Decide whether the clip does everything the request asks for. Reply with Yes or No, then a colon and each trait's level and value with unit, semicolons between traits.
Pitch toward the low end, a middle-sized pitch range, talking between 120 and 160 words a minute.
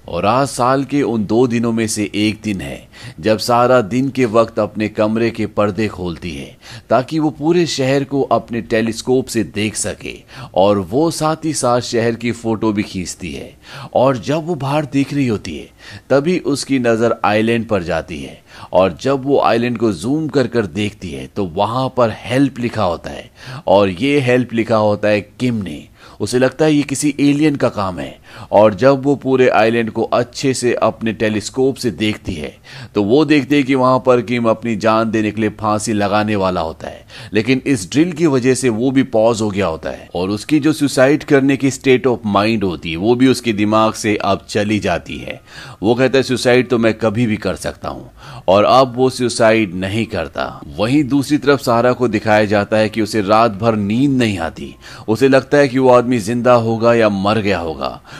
Yes: low, 115 Hz; average, 3.8 semitones; average, 145 wpm